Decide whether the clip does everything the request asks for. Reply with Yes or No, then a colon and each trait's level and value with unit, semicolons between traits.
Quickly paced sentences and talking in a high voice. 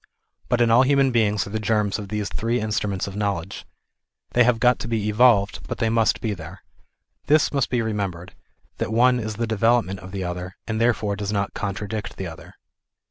No: fast, 210 wpm; low, 110 Hz